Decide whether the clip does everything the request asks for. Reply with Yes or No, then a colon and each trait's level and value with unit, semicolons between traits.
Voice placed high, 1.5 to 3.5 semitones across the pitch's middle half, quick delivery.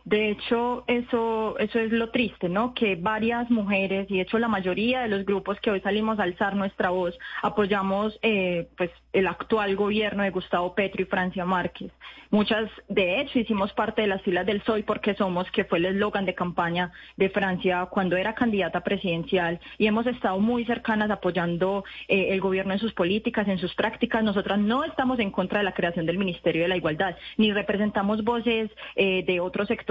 Yes: high, 205 Hz; average, 2.9 semitones; fast, 195 wpm